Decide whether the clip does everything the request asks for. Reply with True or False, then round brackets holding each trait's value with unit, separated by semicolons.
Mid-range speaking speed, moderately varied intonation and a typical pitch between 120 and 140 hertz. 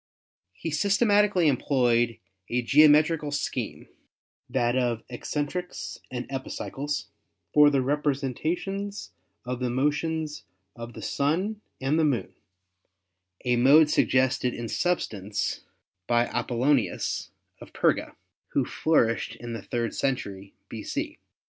False (115 wpm; 4.4 semitones; 135 Hz)